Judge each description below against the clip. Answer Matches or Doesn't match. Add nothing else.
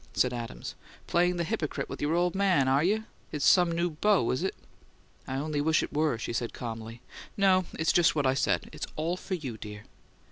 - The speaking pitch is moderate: Matches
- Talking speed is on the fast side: Matches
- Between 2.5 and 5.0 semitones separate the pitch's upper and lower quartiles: Doesn't match